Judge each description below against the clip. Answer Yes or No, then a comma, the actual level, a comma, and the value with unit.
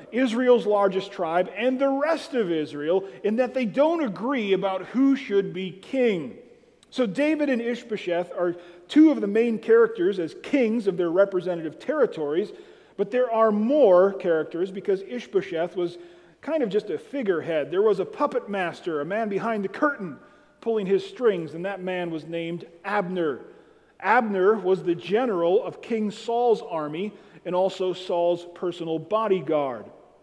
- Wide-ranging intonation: Yes, wide, 6.3 semitones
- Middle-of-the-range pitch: No, high, 205 Hz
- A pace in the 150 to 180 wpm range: Yes, average, 155 wpm